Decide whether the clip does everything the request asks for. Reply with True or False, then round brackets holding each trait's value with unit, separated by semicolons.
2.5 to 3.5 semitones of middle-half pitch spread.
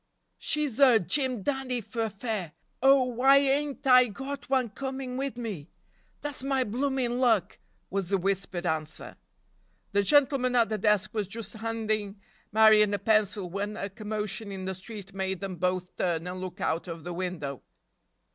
False (5.0 semitones)